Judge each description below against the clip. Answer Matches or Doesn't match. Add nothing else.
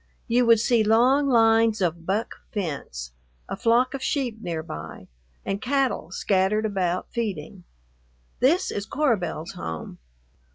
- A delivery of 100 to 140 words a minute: Matches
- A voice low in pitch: Doesn't match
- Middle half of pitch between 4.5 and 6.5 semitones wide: Matches